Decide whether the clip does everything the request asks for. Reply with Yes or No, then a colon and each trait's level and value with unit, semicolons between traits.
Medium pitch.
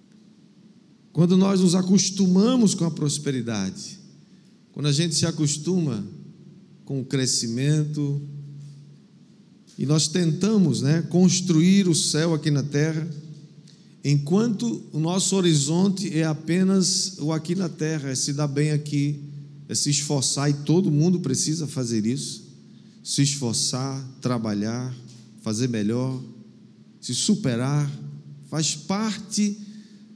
Yes: medium, 155 Hz